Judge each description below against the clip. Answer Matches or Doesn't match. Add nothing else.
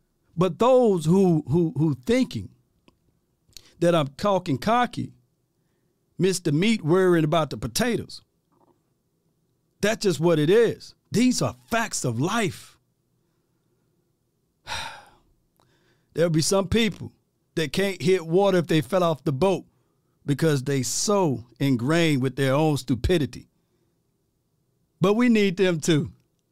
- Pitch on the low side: Doesn't match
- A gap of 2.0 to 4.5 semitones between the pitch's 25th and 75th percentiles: Doesn't match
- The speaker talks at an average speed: Doesn't match